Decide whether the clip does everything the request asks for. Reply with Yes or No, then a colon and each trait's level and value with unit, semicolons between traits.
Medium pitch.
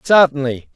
Yes: medium, 145 Hz